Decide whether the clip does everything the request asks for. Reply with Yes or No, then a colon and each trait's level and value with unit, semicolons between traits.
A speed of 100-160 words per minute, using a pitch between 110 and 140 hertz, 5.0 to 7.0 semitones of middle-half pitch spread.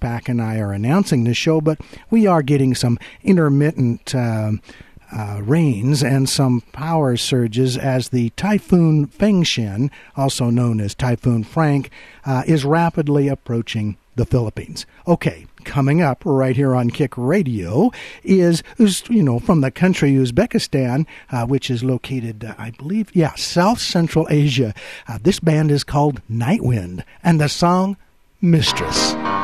Yes: average, 145 wpm; low, 135 Hz; average, 5.3 semitones